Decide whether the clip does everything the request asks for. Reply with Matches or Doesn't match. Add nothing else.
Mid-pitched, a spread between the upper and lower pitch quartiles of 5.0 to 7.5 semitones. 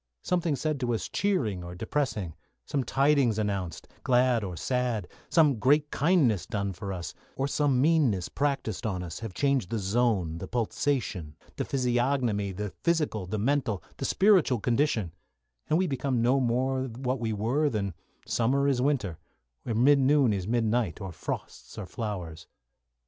Doesn't match